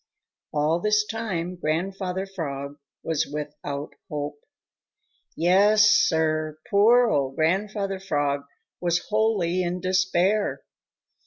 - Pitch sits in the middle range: Yes, medium, 175 Hz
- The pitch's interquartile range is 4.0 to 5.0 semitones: Yes, average, 4.5 semitones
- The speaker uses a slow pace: Yes, slow, 95 wpm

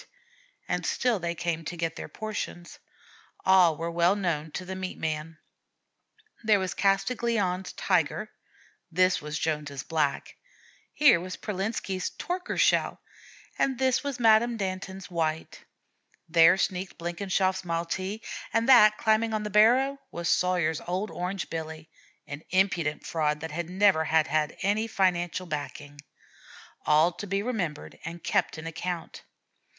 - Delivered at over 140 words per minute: No, slow, 135 wpm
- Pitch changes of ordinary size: Yes, average, 4.1 semitones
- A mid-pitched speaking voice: Yes, medium, 180 Hz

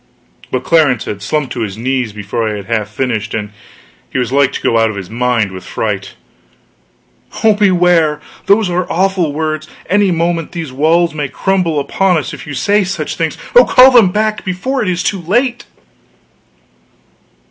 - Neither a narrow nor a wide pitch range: No, wide, 7.4 semitones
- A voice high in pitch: No, medium, 155 Hz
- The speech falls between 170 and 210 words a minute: Yes, average, 180 wpm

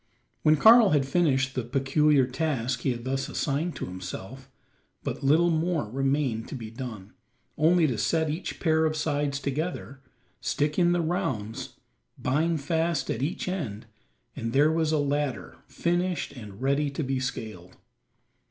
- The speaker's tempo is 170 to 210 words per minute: No, average, 155 wpm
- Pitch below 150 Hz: Yes, medium, 140 Hz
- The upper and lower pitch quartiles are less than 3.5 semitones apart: No, average, 3.8 semitones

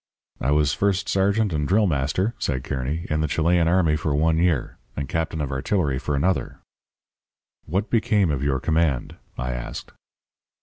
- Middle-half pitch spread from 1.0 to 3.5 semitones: No, average, 4.6 semitones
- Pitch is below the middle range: Yes, very low, 80 Hz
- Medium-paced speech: Yes, average, 165 wpm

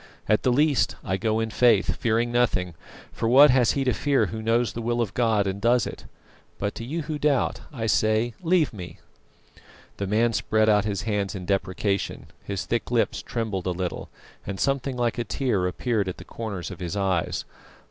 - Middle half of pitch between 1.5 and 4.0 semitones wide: Yes, average, 3.5 semitones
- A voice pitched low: Yes, low, 110 Hz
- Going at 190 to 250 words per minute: Yes, average, 200 wpm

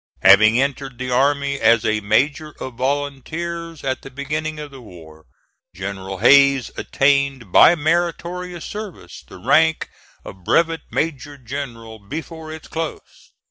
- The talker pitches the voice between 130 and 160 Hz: Yes, medium, 140 Hz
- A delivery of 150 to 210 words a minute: No, slow, 135 wpm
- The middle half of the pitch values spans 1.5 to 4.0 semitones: No, average, 5.3 semitones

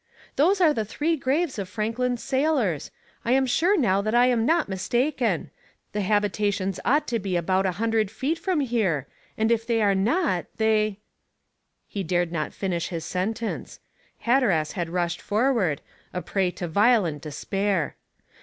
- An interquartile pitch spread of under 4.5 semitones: No, average, 5.2 semitones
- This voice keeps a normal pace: Yes, average, 165 wpm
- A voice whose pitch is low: No, high, 215 Hz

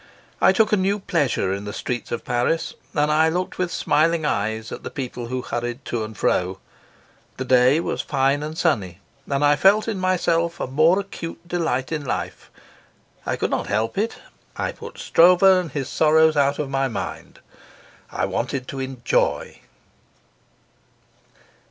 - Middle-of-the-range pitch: Yes, medium, 145 Hz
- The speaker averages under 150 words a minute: No, average, 165 wpm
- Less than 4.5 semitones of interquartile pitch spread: No, wide, 5.4 semitones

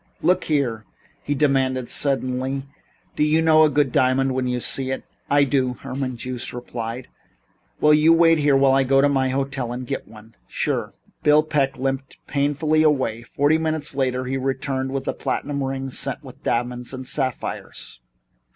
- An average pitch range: No, narrow, 2.1 semitones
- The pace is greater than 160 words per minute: Yes, average, 170 wpm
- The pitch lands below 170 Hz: Yes, low, 135 Hz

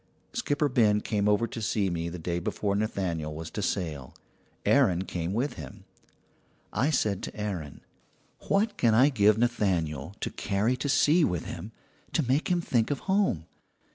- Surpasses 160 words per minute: Yes, average, 170 wpm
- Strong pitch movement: Yes, wide, 6.9 semitones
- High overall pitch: No, low, 105 Hz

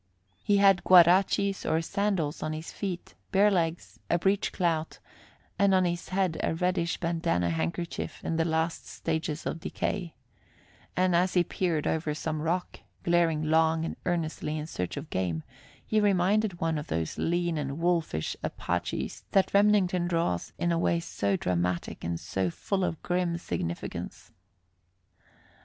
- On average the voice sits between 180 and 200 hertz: No, medium, 170 Hz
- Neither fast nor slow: Yes, average, 150 wpm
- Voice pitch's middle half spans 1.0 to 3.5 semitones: Yes, average, 2.8 semitones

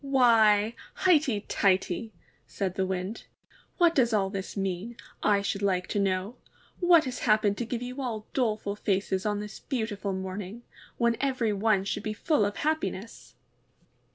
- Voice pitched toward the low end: No, high, 215 Hz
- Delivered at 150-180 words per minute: Yes, average, 155 wpm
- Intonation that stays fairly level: No, average, 3.5 semitones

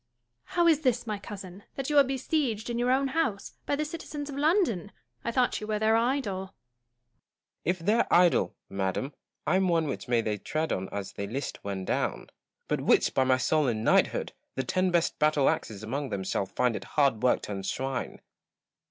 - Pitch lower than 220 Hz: Yes, medium, 185 Hz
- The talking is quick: Yes, fast, 215 wpm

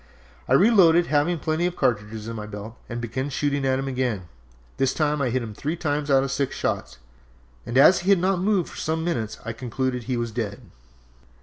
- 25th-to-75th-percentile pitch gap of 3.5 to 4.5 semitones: No, average, 5.2 semitones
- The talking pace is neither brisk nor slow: No, fast, 215 wpm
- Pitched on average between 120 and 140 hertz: Yes, low, 135 Hz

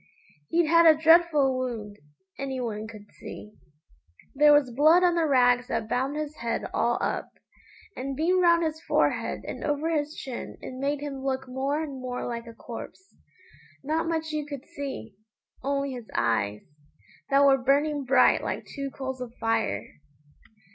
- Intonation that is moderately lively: Yes, average, 3.6 semitones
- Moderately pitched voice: No, very high, 275 Hz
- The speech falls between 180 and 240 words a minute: No, average, 165 wpm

